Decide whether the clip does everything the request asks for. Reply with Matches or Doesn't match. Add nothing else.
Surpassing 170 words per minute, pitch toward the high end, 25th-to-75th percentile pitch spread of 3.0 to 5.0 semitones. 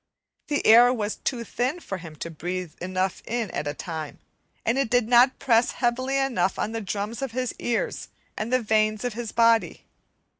Matches